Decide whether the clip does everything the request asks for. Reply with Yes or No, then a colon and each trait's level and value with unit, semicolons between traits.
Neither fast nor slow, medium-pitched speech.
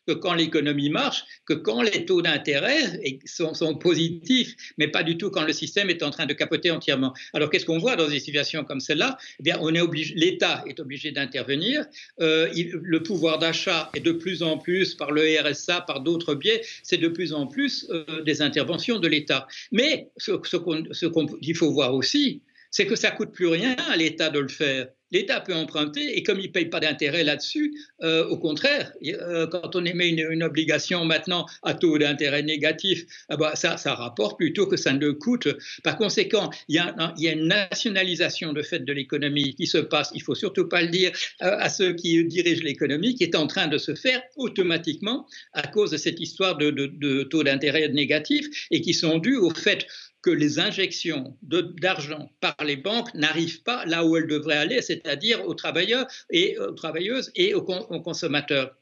Yes: average, 205 wpm; medium, 165 Hz